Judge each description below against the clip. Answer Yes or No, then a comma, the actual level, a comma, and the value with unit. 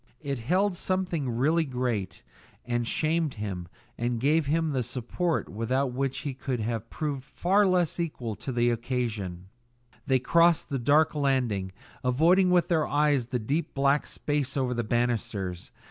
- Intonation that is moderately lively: Yes, average, 4.8 semitones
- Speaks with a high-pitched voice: No, low, 130 Hz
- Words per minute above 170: No, average, 155 wpm